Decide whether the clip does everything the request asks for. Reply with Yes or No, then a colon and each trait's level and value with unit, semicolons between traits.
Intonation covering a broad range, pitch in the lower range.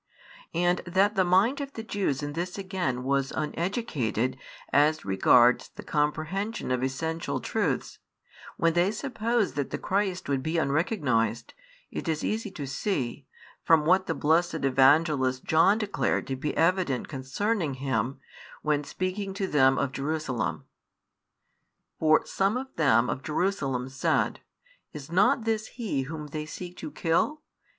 No: wide, 6.0 semitones; medium, 160 Hz